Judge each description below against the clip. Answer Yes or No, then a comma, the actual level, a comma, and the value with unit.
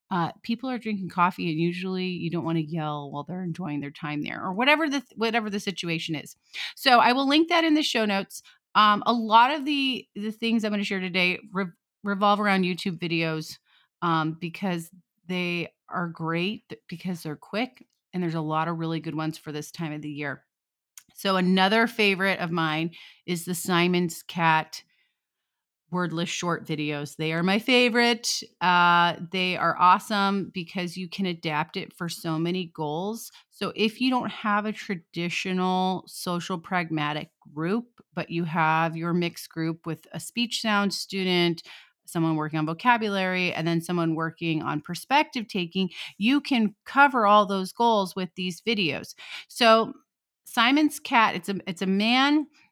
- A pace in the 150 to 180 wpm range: Yes, average, 175 wpm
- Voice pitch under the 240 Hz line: Yes, medium, 185 Hz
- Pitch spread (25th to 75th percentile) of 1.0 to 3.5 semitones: No, average, 4.6 semitones